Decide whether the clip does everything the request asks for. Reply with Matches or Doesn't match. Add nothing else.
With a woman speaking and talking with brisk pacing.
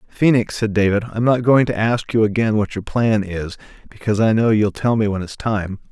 Doesn't match